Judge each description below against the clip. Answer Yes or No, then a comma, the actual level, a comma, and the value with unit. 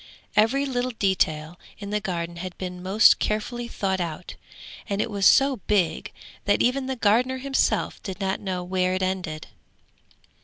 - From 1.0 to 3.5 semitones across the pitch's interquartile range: No, average, 4.6 semitones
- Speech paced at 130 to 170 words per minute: Yes, average, 160 wpm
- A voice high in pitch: Yes, high, 195 Hz